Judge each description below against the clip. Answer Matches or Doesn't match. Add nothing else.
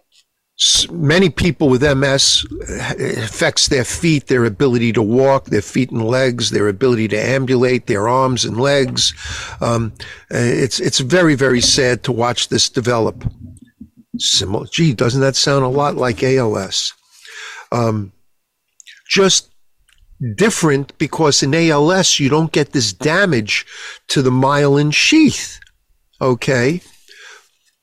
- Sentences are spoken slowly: Matches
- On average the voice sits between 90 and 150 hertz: Matches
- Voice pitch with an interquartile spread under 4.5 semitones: Matches